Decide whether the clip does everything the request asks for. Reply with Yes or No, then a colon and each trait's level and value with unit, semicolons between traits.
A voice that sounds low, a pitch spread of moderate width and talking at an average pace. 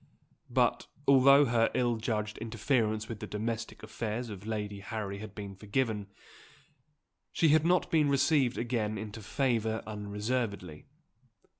No: low, 110 Hz; average, 3.0 semitones; slow, 130 wpm